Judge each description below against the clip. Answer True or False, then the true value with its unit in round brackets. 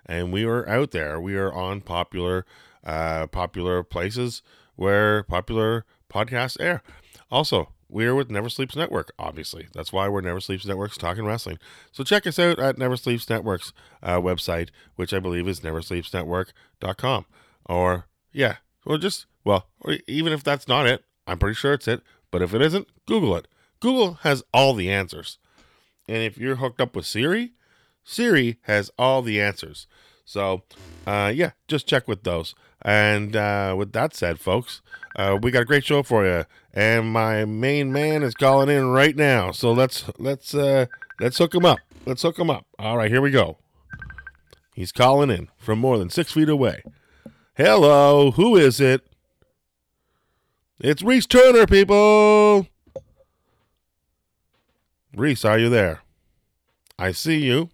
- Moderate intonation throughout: False (6.9 semitones)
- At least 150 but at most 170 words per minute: True (165 wpm)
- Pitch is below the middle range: True (115 Hz)